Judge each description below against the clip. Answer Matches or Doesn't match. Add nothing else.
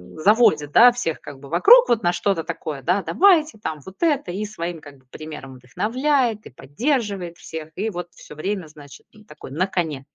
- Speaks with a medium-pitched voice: Matches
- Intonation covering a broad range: Matches